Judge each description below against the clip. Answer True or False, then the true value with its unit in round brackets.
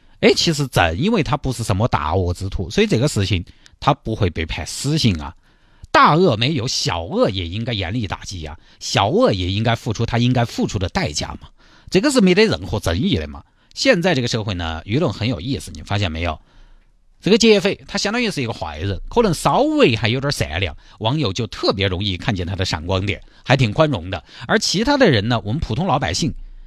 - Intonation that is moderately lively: False (7.2 semitones)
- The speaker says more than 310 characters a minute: True (320 characters per minute)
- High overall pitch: False (115 Hz)